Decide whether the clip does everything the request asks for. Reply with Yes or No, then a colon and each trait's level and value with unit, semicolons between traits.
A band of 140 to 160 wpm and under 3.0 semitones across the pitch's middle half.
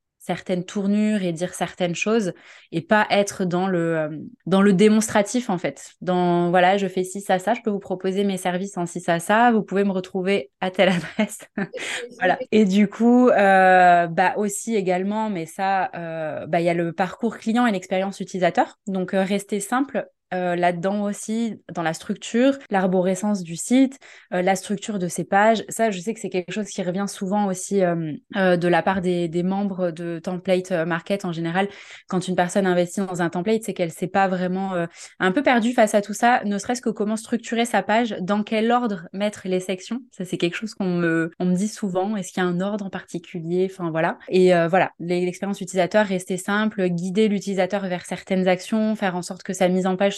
No: average, 210 wpm; narrow, 2.5 semitones